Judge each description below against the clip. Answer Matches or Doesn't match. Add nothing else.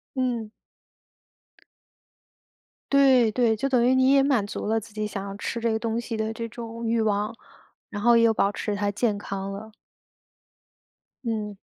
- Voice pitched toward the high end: Matches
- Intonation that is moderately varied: Doesn't match